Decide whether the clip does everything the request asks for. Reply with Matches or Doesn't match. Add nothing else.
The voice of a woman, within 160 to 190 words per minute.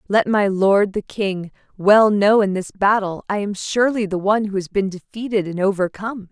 Doesn't match